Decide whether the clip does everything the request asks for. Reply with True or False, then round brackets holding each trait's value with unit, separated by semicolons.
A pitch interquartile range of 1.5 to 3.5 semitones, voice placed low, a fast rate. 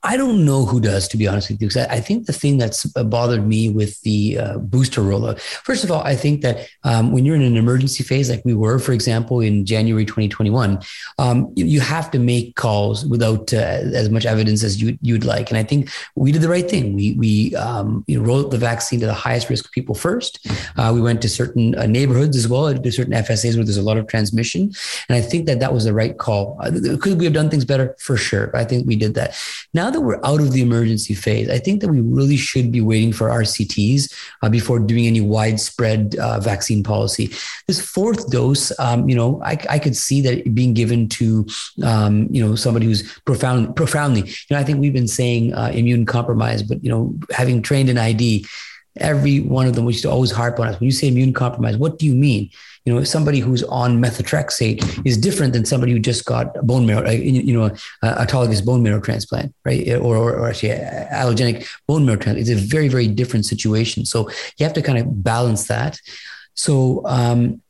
True (3.2 semitones; 120 Hz; 220 wpm)